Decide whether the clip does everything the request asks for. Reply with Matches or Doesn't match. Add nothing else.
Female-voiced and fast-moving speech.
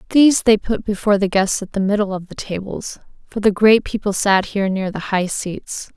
Matches